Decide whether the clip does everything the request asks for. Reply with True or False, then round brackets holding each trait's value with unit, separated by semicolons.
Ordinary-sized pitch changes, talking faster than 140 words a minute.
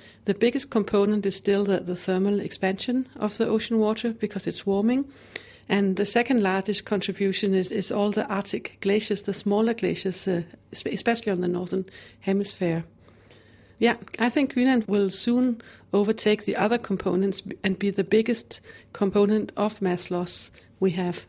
False (2.3 semitones; 160 wpm)